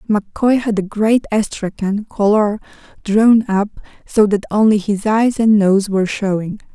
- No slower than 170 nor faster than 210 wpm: No, average, 150 wpm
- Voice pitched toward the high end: Yes, high, 210 Hz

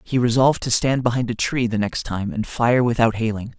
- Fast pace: Yes, fast, 235 wpm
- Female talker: No, male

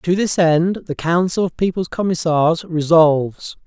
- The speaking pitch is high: No, medium, 170 Hz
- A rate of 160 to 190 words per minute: No, average, 145 wpm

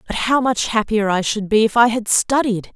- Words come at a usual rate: No, fast, 240 wpm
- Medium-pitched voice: No, high, 220 Hz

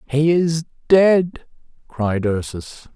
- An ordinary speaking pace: No, slow, 100 wpm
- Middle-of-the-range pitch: Yes, medium, 145 Hz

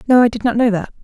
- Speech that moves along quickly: Yes, fast, 350 wpm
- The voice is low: No, high, 230 Hz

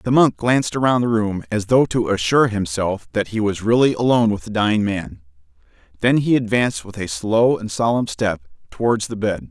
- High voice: No, low, 110 Hz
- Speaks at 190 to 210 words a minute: Yes, average, 200 wpm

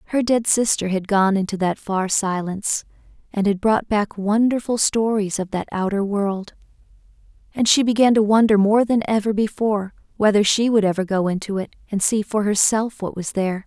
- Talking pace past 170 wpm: Yes, average, 185 wpm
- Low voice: No, high, 205 Hz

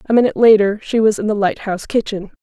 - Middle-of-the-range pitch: No, high, 210 Hz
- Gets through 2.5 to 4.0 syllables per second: No, 6.8 syllables/s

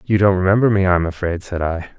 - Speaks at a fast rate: Yes, fast, 270 wpm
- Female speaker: No, male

